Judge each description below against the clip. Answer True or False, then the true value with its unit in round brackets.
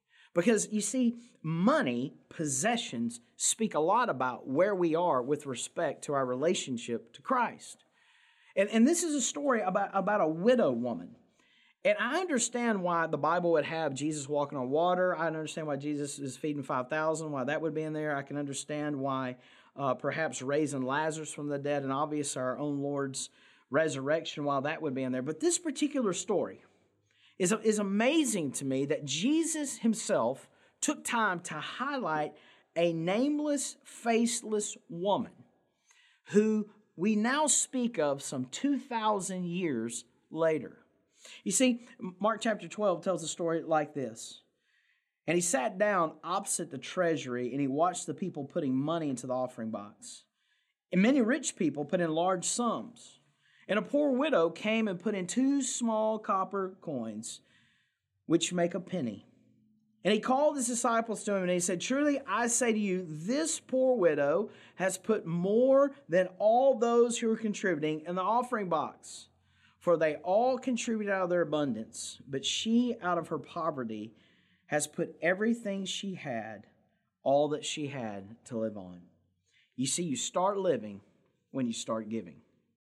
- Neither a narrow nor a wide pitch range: False (7.8 semitones)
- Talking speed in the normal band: True (160 wpm)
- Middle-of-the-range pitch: True (180 Hz)